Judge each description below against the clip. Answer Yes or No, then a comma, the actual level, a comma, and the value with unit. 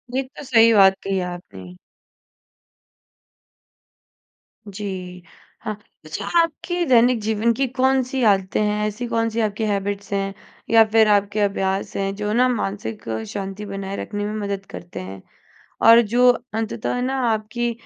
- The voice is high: Yes, high, 210 Hz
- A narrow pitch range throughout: No, average, 3.0 semitones